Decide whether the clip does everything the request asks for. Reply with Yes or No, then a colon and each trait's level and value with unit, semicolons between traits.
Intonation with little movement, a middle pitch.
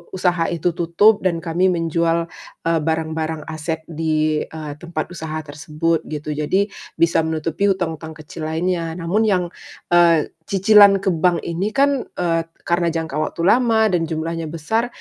Yes: narrow, 2.3 semitones; medium, 165 Hz